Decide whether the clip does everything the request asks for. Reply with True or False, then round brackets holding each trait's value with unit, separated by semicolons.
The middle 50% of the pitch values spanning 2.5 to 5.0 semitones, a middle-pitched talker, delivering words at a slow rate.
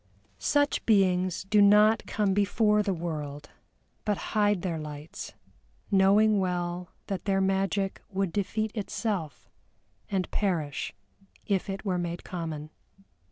False (3.0 semitones; 195 Hz; 120 wpm)